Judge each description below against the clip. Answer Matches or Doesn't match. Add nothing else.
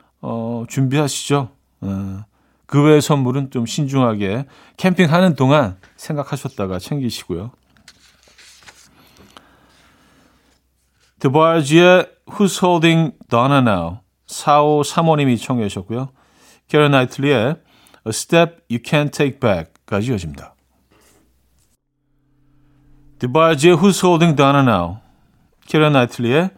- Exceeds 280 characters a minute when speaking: Matches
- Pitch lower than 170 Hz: Matches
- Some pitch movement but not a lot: Matches